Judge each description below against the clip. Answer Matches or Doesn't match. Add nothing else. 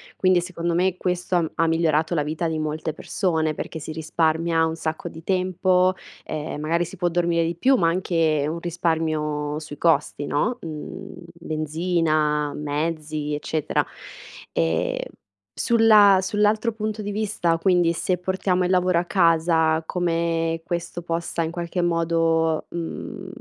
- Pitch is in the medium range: Matches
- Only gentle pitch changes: Matches